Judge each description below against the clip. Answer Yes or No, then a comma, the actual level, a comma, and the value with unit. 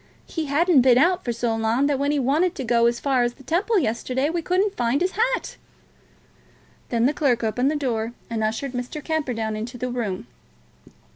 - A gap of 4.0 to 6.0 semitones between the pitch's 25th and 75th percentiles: Yes, average, 4.9 semitones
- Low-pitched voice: No, very high, 260 Hz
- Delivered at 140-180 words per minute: No, average, 200 wpm